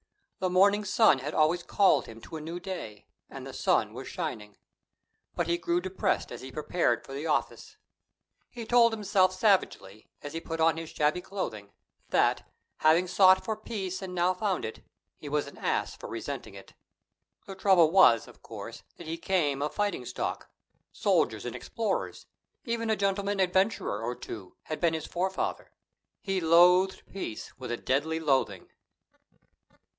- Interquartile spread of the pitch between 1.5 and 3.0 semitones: No, average, 4.2 semitones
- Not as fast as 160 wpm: No, average, 170 wpm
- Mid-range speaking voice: Yes, medium, 175 Hz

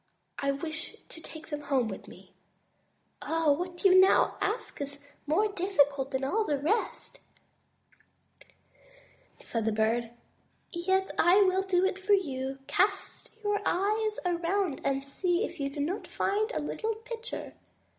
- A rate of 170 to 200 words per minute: No, average, 150 wpm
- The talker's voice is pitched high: Yes, very high, 345 Hz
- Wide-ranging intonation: Yes, wide, 5.9 semitones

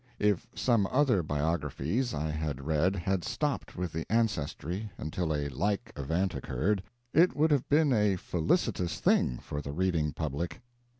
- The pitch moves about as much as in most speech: No, wide, 5.8 semitones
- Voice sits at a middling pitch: No, very low, 90 Hz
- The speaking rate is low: No, average, 155 wpm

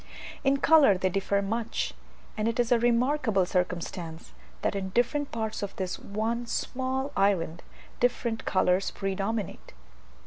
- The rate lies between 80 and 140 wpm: Yes, slow, 135 wpm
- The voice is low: No, high, 215 Hz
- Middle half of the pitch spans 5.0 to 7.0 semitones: No, average, 4.1 semitones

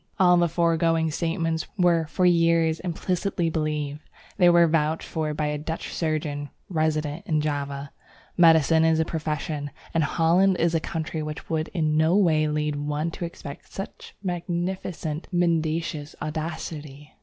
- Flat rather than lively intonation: Yes, narrow, 1.9 semitones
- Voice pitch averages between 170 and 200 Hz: No, medium, 160 Hz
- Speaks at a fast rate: No, average, 145 wpm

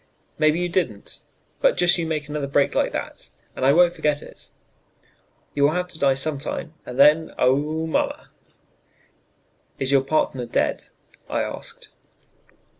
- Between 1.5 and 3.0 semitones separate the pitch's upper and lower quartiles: Yes, average, 2.7 semitones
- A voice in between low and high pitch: Yes, medium, 150 Hz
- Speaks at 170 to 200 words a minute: No, average, 150 wpm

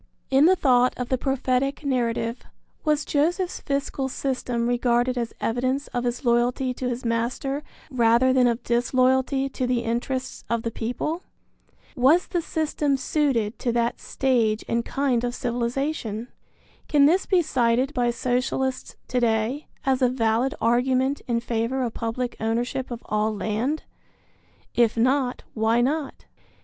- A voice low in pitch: No, very high, 250 Hz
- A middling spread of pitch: No, narrow, 2.3 semitones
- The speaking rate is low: No, average, 145 wpm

